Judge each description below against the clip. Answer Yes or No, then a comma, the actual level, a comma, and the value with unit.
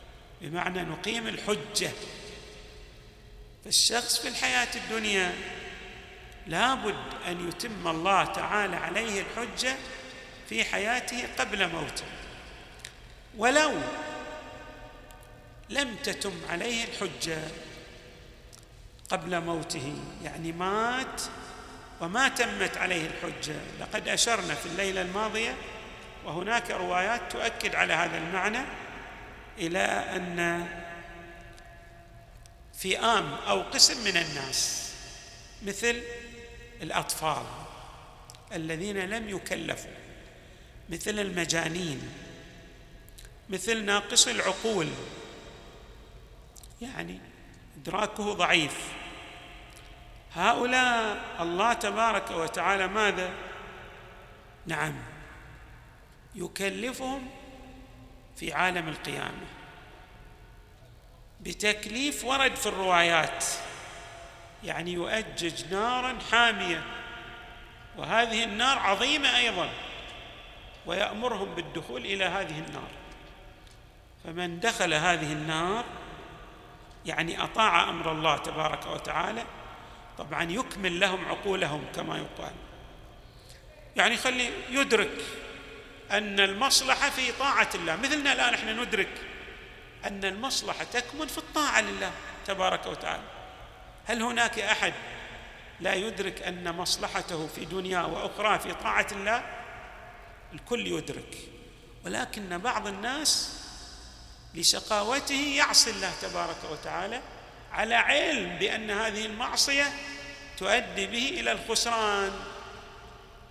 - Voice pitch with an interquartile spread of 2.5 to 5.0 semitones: No, wide, 5.6 semitones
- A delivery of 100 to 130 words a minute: No, average, 85 wpm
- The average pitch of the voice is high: Yes, high, 195 Hz